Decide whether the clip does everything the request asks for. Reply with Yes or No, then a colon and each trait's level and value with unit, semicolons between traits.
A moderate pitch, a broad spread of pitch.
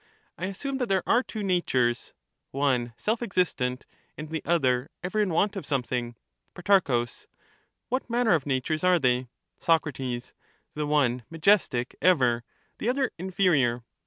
Yes: medium, 160 Hz; wide, 7.4 semitones